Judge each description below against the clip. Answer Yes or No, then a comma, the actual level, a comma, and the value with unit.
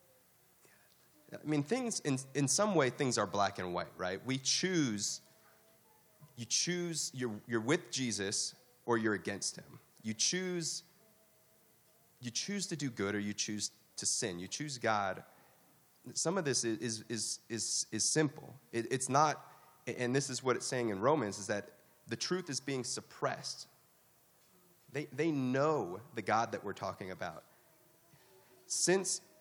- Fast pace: No, average, 155 wpm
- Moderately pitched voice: No, low, 130 Hz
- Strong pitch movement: Yes, wide, 6.0 semitones